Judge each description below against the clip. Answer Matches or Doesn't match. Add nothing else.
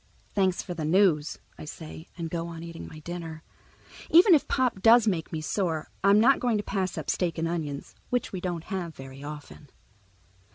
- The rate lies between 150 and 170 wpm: Doesn't match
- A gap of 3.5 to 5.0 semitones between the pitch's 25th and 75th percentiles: Matches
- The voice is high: Doesn't match